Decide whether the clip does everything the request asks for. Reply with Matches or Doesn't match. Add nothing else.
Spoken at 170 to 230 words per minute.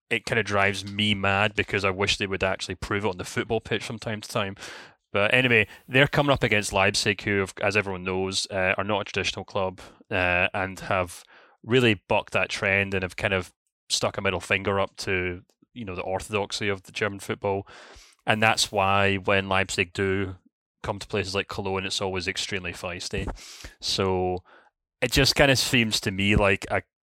Matches